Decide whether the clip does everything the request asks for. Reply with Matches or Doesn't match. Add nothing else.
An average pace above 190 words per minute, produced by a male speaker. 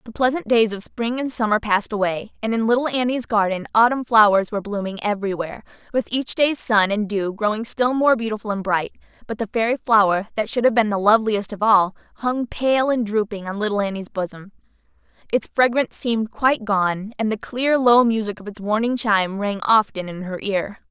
Doesn't match